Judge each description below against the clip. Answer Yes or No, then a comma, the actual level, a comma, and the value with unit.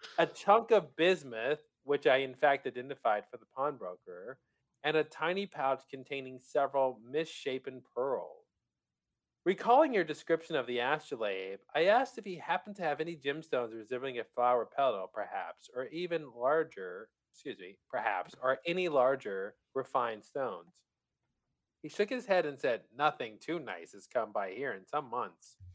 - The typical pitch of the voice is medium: Yes, medium, 155 Hz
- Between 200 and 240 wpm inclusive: No, average, 155 wpm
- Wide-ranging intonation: Yes, wide, 7.4 semitones